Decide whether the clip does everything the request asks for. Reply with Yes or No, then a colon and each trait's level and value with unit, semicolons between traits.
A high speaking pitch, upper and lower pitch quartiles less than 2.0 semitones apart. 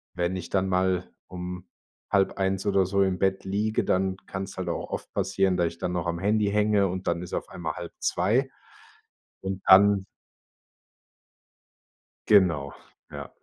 No: very low, 95 Hz; narrow, 1.6 semitones